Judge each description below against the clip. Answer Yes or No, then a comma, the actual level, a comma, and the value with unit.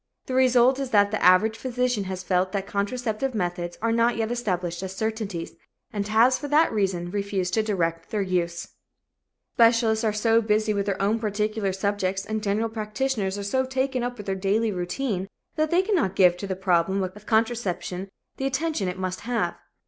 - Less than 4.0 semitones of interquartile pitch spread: Yes, average, 3.6 semitones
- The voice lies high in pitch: Yes, high, 210 Hz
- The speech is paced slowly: No, average, 185 wpm